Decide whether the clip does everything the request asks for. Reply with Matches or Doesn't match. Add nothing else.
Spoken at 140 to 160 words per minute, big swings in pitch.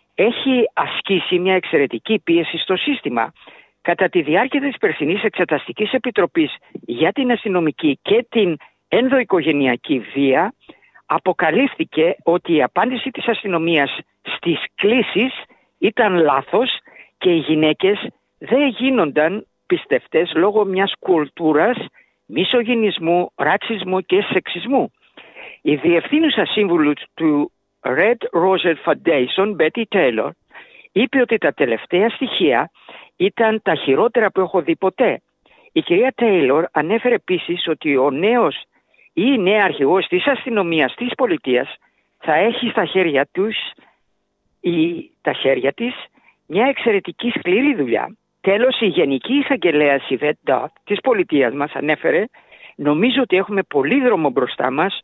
Doesn't match